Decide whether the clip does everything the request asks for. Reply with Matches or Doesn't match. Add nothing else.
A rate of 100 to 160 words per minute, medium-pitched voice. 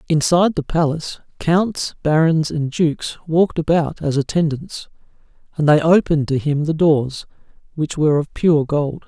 Matches